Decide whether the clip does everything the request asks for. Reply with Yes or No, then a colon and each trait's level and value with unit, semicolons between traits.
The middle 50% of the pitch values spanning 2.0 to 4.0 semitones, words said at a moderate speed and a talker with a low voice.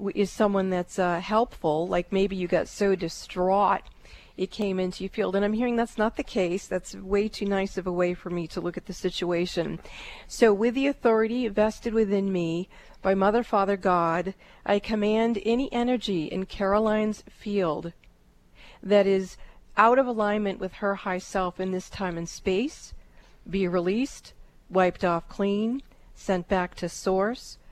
No: average, 2.8 semitones; average, 170 wpm; high, 195 Hz